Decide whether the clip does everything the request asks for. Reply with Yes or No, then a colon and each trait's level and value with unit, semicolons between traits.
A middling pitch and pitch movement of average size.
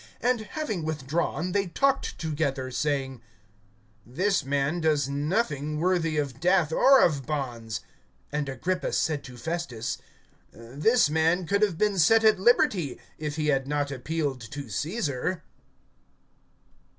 Yes: medium, 155 Hz; average, 4.7 semitones